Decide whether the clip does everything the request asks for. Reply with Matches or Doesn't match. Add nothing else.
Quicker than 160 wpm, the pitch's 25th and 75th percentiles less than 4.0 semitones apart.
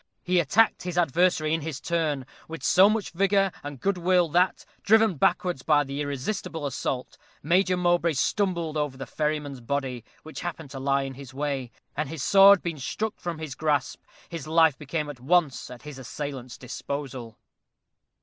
Doesn't match